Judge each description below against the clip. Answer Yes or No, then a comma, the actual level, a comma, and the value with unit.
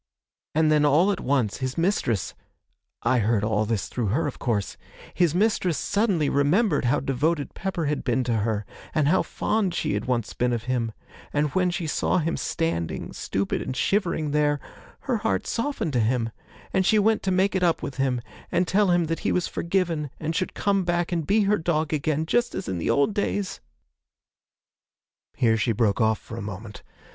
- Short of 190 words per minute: No, average, 195 wpm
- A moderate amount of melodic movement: No, wide, 7.2 semitones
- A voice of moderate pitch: Yes, medium, 150 Hz